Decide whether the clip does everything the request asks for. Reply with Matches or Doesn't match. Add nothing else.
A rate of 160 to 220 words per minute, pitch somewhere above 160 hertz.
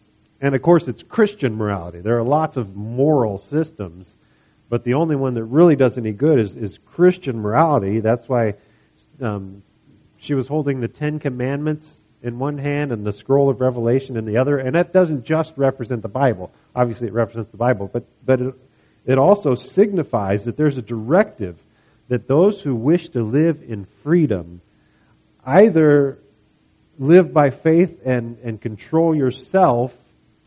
Doesn't match